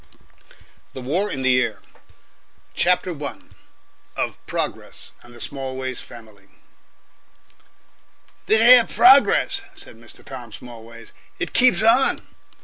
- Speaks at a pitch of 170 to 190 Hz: No, low, 130 Hz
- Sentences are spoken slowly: Yes, slow, 120 wpm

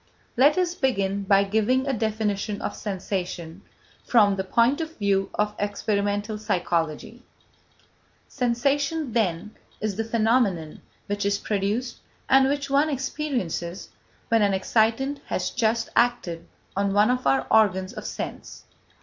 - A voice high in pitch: Yes, high, 215 Hz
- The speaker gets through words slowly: Yes, slow, 130 wpm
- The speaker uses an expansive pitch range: No, average, 4.2 semitones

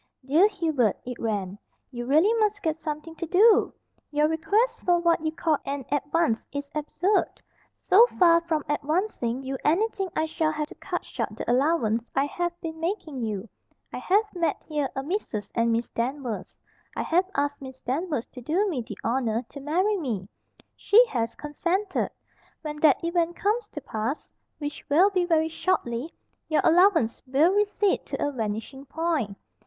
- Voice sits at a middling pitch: No, very high, 305 Hz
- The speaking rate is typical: Yes, average, 170 wpm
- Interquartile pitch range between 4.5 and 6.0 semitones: Yes, average, 5.1 semitones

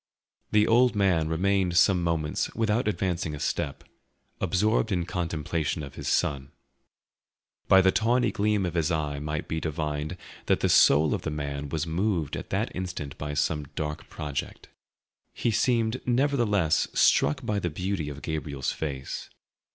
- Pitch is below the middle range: Yes, very low, 85 Hz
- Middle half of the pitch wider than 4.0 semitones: Yes, average, 4.9 semitones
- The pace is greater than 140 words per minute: Yes, average, 155 wpm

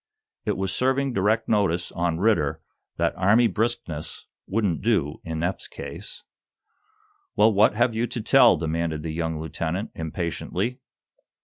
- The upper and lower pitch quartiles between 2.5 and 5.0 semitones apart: No, wide, 5.6 semitones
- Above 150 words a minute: No, slow, 135 wpm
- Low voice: Yes, very low, 95 Hz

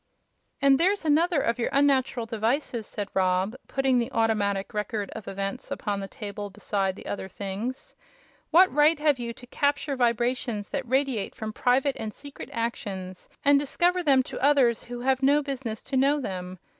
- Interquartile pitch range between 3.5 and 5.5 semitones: Yes, average, 5.1 semitones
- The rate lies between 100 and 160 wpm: No, average, 170 wpm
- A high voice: Yes, high, 245 Hz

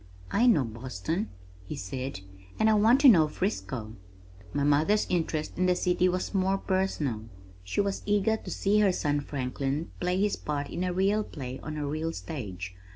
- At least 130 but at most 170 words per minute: No, average, 180 wpm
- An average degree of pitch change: No, wide, 6.2 semitones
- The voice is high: No, medium, 165 Hz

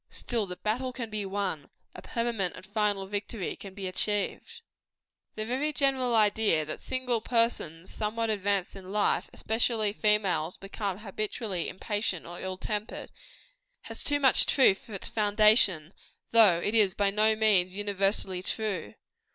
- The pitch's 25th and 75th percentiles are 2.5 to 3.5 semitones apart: Yes, average, 2.8 semitones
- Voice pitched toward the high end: Yes, high, 210 Hz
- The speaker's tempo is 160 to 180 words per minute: No, average, 150 wpm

